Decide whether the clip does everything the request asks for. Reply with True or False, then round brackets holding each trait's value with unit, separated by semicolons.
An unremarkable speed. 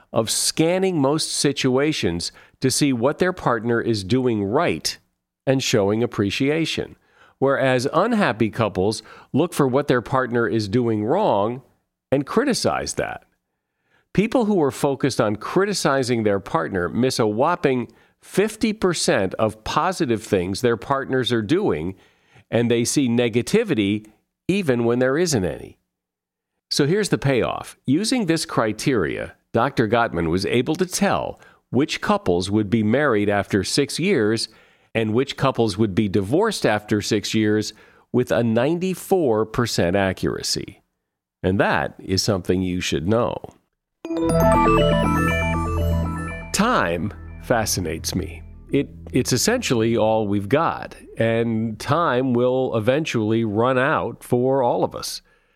False (125 wpm)